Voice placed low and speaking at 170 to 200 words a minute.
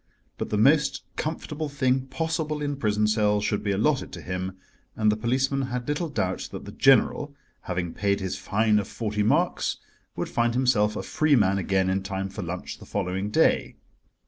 Yes: low, 110 Hz; average, 185 wpm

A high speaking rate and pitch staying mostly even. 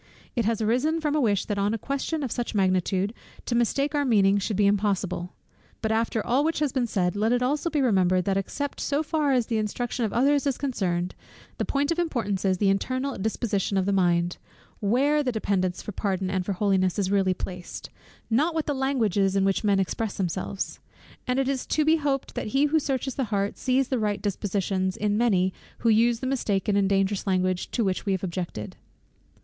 No: fast, 215 wpm; wide, 5.4 semitones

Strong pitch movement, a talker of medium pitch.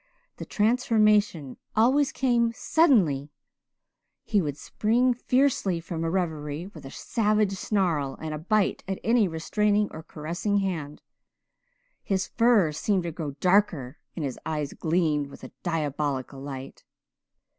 Yes: wide, 6.0 semitones; medium, 180 Hz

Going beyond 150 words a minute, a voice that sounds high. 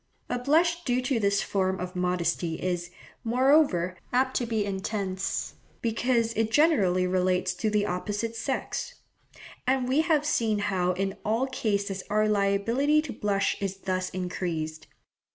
No: average, 145 wpm; high, 205 Hz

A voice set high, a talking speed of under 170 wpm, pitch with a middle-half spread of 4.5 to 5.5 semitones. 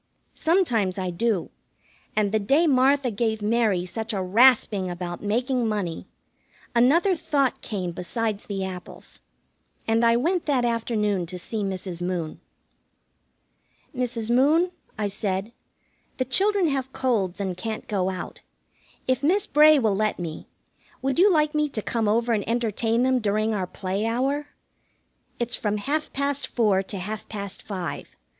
Yes: high, 225 Hz; average, 150 wpm; average, 5.0 semitones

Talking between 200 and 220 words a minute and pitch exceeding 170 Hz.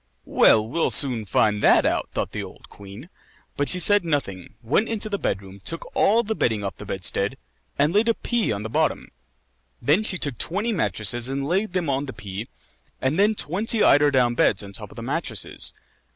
No: fast, 205 wpm; medium, 140 Hz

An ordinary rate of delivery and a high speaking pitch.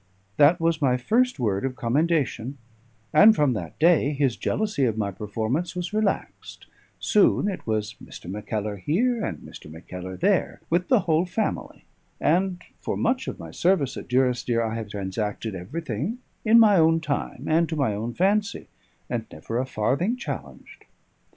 No: average, 165 wpm; medium, 140 Hz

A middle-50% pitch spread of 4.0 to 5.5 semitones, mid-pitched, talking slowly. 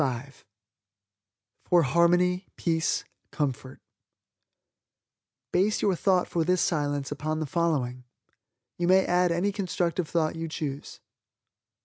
No: average, 3.1 semitones; medium, 170 Hz; slow, 105 wpm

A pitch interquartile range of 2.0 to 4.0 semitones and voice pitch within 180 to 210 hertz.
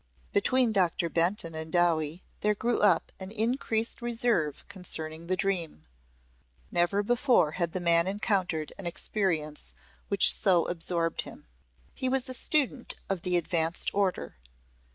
No: average, 4.6 semitones; medium, 185 Hz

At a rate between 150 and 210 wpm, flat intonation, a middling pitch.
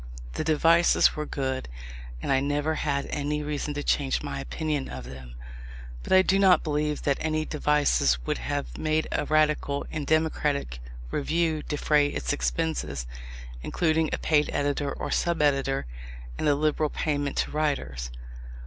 Yes: average, 155 wpm; narrow, 2.0 semitones; medium, 150 Hz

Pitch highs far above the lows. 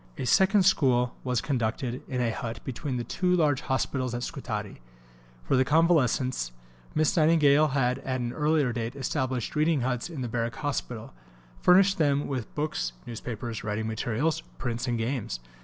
No: average, 4.1 semitones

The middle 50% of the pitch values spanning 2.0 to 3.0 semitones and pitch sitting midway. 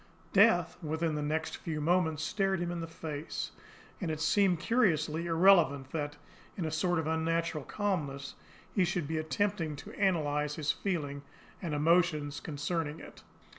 Yes: average, 2.7 semitones; medium, 160 Hz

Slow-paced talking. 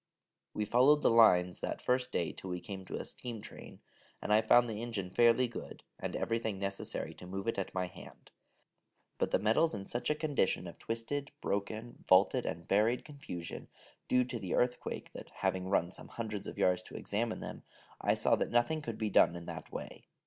No: average, 200 wpm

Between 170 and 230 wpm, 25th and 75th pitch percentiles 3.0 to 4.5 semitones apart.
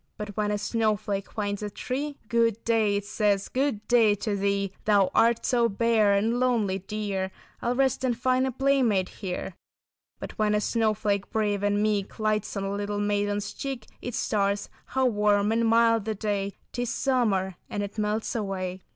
No: average, 175 wpm; narrow, 2.4 semitones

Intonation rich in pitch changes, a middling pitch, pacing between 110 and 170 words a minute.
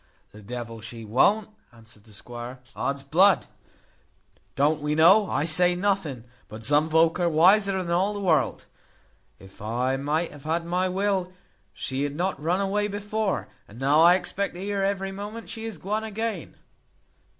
Yes: wide, 6.4 semitones; medium, 170 Hz; average, 165 wpm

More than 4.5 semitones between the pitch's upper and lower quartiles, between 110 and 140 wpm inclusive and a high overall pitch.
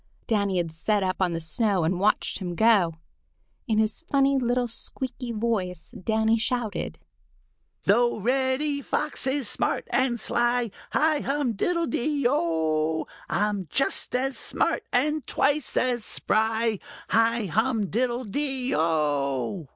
Yes: wide, 5.4 semitones; slow, 135 wpm; high, 230 Hz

